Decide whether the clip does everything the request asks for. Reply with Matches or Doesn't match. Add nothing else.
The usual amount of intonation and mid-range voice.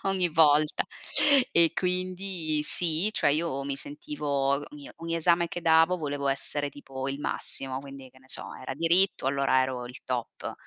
Matches